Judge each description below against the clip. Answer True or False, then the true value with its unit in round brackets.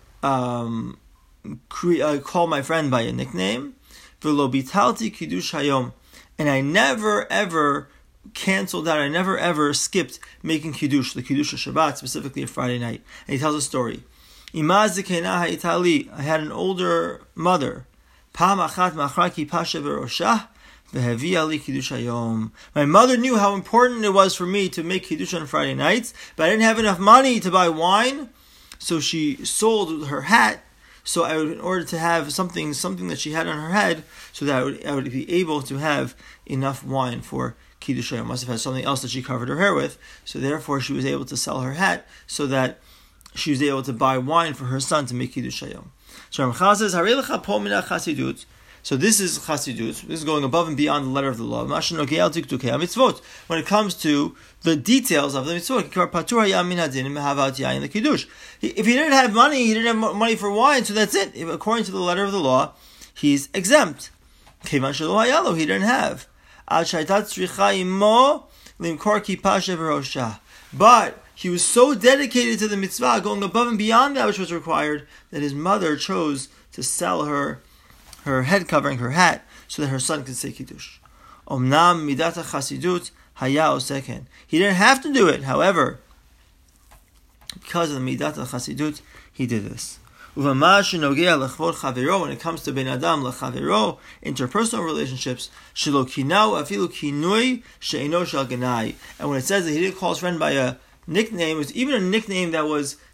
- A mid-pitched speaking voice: True (160 Hz)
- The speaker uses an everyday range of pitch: False (6.1 semitones)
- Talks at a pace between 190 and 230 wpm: False (165 wpm)